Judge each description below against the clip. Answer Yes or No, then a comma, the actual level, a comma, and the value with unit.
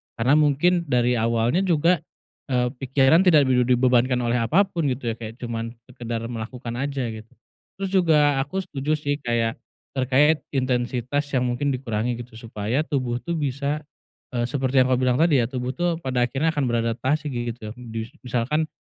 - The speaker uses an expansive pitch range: No, average, 3.5 semitones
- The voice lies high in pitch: No, low, 130 Hz